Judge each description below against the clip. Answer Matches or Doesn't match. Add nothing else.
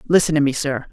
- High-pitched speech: Doesn't match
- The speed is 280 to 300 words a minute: Doesn't match